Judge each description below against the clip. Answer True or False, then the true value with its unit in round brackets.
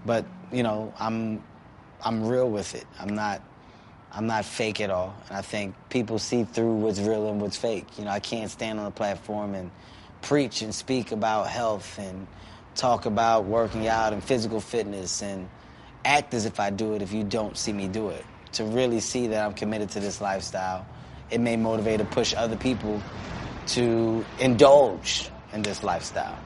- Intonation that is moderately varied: False (2.2 semitones)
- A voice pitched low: True (110 Hz)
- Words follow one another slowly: False (190 wpm)